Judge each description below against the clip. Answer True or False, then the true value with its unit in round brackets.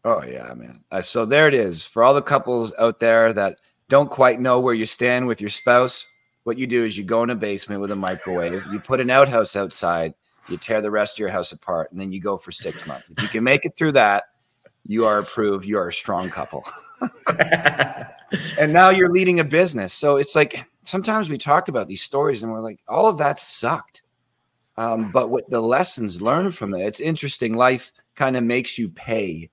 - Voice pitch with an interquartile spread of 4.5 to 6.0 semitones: True (4.8 semitones)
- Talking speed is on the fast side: True (220 wpm)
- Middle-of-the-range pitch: False (120 Hz)